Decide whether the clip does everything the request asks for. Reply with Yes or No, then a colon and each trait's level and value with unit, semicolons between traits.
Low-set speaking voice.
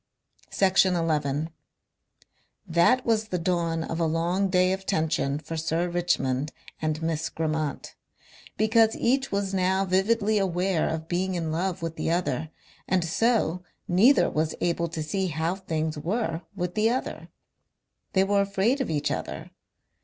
No: medium, 175 Hz